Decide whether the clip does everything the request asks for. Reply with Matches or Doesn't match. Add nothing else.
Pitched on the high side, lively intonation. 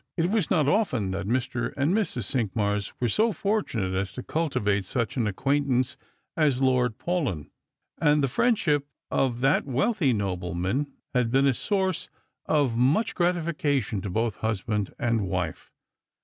Doesn't match